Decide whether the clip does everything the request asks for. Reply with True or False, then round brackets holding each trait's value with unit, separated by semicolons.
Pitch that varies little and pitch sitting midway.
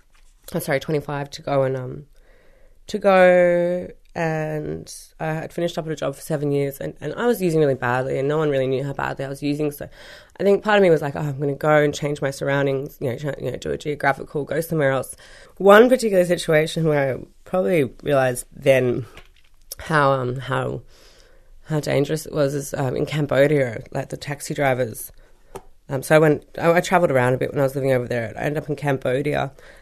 False (3.4 semitones; 145 Hz)